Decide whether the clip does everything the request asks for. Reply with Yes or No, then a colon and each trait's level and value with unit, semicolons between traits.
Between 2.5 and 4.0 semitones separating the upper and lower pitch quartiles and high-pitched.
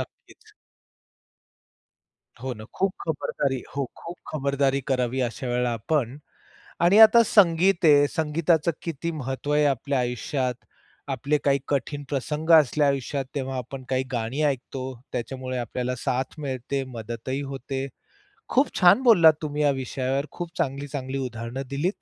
No: average, 2.9 semitones; medium, 140 Hz